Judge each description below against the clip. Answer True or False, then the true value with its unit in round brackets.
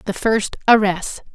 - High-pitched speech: True (210 Hz)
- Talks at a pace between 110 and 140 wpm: True (135 wpm)